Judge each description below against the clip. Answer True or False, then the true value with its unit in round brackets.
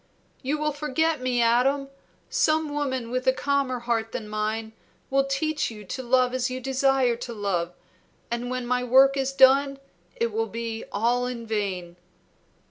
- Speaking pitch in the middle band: False (250 Hz)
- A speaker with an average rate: True (165 wpm)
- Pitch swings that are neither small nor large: True (3.0 semitones)